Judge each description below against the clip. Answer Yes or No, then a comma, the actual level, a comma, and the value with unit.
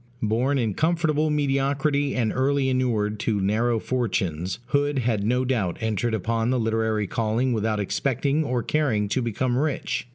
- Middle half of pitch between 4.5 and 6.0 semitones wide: No, average, 4.0 semitones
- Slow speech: No, average, 155 wpm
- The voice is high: No, low, 120 Hz